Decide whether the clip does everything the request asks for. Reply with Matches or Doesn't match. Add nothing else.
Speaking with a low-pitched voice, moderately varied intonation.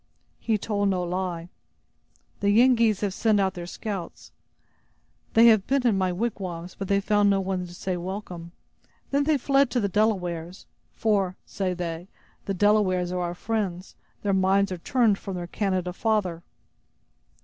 Doesn't match